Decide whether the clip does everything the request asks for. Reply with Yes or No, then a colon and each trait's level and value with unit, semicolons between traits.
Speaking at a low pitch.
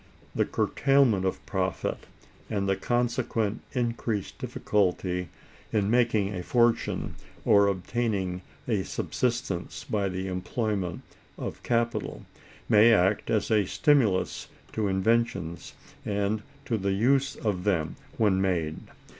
Yes: low, 105 Hz